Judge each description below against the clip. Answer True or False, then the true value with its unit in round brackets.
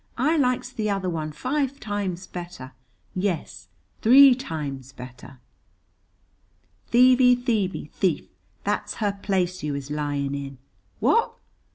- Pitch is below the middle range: False (190 Hz)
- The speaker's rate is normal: False (120 wpm)